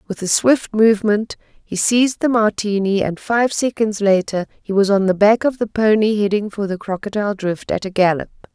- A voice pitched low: No, high, 205 Hz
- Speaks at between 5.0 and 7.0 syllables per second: Yes, 5.2 syllables/s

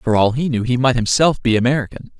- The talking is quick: Yes, fast, 245 wpm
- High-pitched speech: No, low, 125 Hz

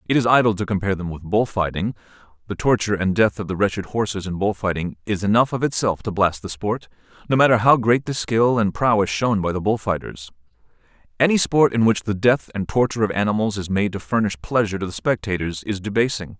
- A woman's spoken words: No, male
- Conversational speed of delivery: No, fast, 225 wpm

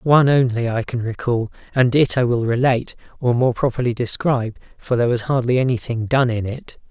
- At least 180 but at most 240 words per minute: Yes, average, 190 wpm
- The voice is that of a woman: No, male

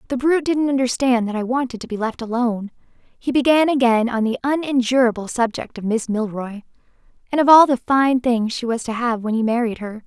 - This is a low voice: No, high, 245 Hz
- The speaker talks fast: Yes, fast, 210 wpm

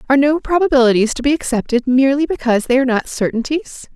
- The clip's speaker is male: No, female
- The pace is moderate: Yes, average, 180 wpm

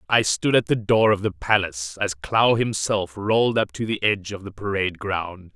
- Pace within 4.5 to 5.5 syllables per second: Yes, 5.1 syllables/s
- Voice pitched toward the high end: No, low, 100 Hz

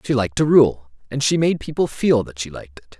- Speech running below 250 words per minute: No, fast, 260 wpm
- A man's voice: Yes, male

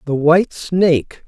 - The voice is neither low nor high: Yes, medium, 165 Hz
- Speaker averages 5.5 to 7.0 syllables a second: No, 4.4 syllables/s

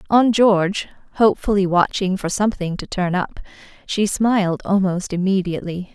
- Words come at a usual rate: No, slow, 130 wpm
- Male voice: No, female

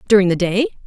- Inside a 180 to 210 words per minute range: Yes, fast, 205 wpm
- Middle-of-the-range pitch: No, high, 200 Hz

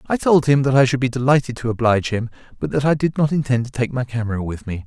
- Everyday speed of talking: No, fast, 285 wpm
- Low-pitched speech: Yes, low, 125 Hz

